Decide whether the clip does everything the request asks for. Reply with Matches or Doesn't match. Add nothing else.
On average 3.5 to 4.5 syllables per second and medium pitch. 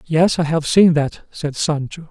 Matches